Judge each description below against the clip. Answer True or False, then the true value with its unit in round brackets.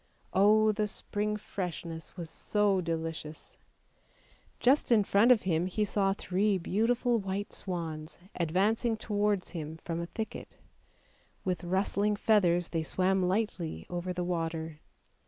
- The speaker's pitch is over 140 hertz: True (190 Hz)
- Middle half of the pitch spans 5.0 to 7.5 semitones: False (3.7 semitones)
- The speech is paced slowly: True (130 wpm)